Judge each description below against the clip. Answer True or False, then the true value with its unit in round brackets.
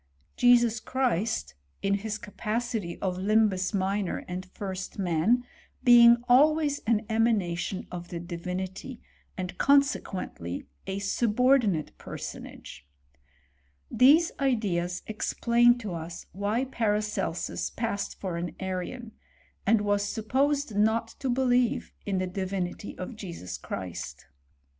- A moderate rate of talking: False (120 wpm)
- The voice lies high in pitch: True (205 Hz)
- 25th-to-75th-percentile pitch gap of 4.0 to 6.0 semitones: True (4.6 semitones)